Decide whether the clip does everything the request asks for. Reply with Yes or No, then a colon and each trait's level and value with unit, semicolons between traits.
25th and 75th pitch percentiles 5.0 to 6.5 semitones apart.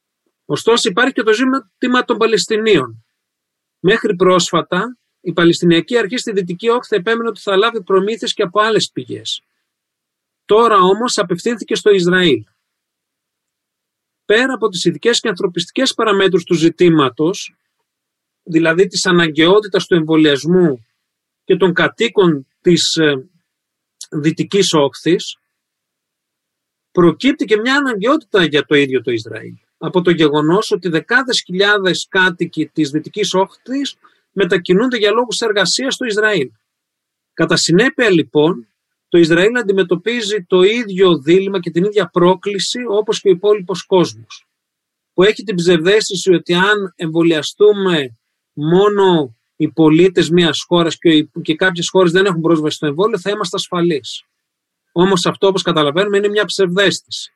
No: average, 4.2 semitones